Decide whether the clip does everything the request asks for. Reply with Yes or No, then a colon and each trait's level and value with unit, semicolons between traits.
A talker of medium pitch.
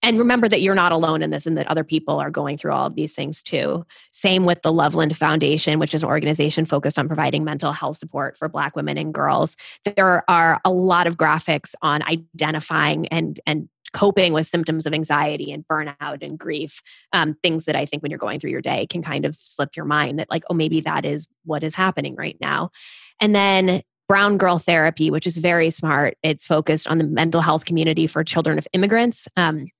Yes: medium, 160 Hz